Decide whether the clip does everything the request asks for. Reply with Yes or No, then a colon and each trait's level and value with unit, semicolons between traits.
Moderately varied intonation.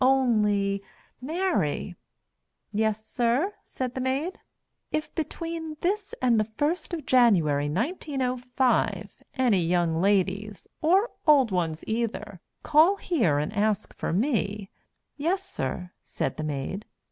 No: wide, 7.5 semitones